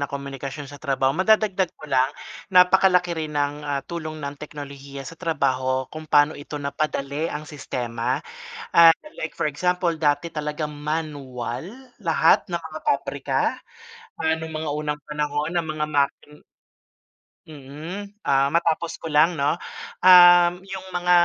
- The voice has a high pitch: No, medium, 150 Hz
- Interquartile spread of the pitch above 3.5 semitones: No, average, 3.1 semitones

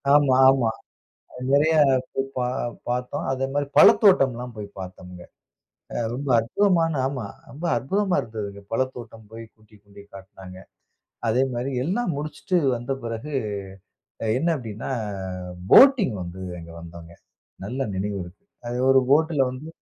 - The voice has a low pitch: Yes, low, 125 Hz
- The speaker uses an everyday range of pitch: No, wide, 6.0 semitones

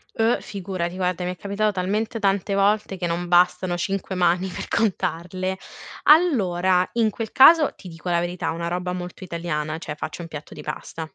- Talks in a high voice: No, medium, 180 Hz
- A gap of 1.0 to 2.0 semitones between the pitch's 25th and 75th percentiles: No, narrow, 2.4 semitones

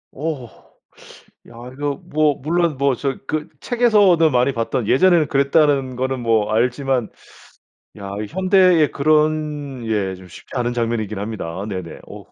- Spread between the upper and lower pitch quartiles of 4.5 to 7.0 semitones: Yes, average, 5.2 semitones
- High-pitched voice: No, low, 135 Hz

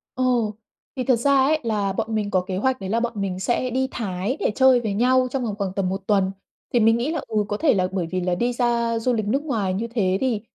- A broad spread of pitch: No, average, 4.3 semitones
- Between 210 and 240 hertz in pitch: Yes, high, 225 Hz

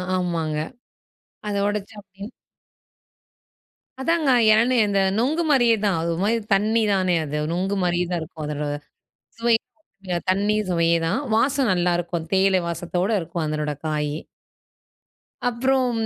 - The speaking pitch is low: No, high, 190 Hz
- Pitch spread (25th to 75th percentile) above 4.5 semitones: Yes, average, 5.2 semitones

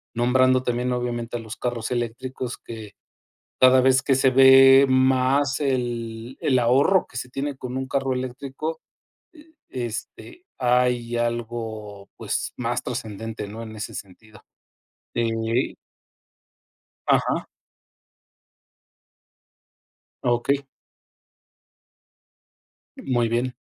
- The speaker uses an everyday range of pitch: No, narrow, 2.0 semitones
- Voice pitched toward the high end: No, low, 125 Hz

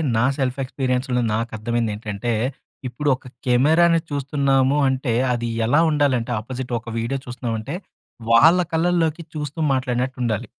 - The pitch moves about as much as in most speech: Yes, average, 3.5 semitones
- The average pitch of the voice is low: Yes, low, 130 Hz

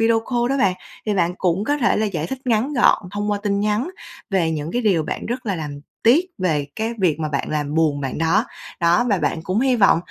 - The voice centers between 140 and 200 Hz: Yes, high, 195 Hz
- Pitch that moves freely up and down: Yes, wide, 5.9 semitones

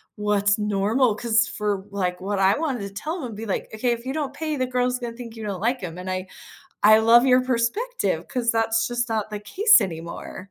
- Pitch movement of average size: Yes, average, 3.6 semitones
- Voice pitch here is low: No, high, 225 Hz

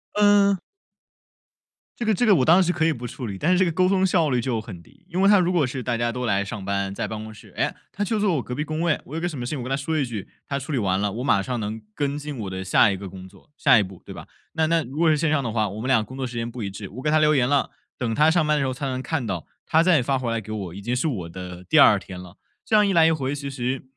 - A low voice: Yes, low, 130 Hz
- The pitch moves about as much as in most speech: No, wide, 6.6 semitones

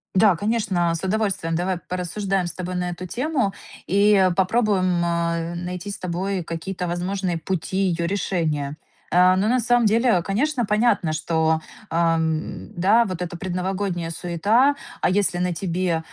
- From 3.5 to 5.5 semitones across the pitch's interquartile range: No, average, 2.9 semitones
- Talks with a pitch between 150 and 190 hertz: Yes, medium, 185 Hz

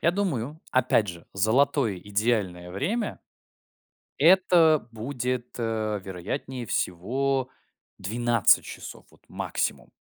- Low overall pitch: Yes, low, 120 Hz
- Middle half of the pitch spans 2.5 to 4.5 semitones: No, average, 5.3 semitones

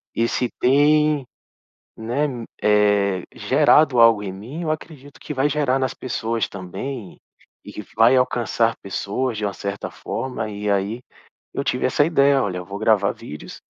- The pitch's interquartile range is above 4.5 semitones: Yes, average, 5.1 semitones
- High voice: No, low, 115 Hz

